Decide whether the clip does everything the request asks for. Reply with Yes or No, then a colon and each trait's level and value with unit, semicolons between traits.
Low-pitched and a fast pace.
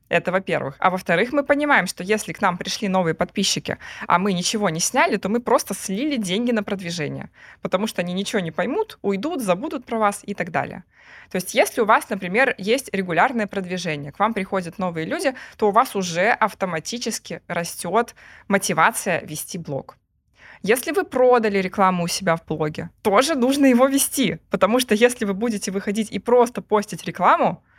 No: high, 200 Hz; fast, 180 wpm